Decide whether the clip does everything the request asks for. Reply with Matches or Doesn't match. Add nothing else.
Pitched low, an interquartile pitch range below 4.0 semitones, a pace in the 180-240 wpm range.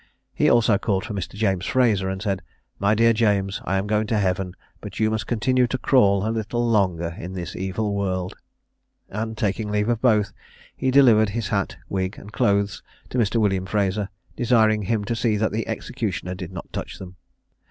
Matches